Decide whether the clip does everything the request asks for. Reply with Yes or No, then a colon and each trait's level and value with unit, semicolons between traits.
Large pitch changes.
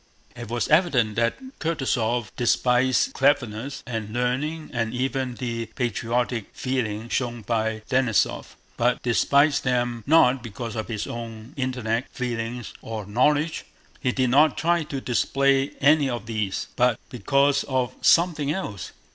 No: average, 3.1 semitones